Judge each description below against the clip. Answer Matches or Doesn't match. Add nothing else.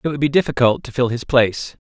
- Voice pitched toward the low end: Matches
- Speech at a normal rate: Doesn't match